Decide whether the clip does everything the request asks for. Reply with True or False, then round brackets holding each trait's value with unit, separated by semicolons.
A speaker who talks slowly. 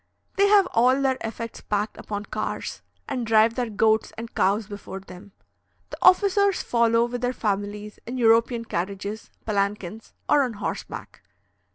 False (150 wpm)